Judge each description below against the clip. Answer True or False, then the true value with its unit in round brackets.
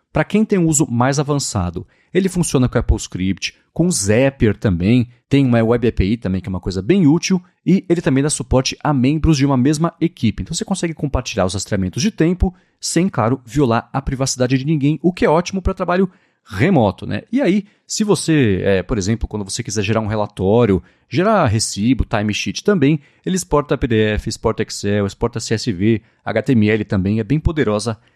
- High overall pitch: False (125 Hz)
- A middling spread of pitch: False (7.0 semitones)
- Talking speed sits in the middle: False (190 wpm)